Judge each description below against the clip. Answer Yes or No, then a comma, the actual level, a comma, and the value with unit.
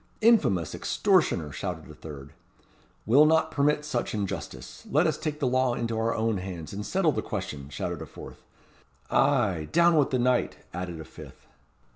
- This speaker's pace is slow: No, average, 170 wpm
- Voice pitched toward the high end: No, low, 120 Hz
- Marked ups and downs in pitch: Yes, wide, 8.7 semitones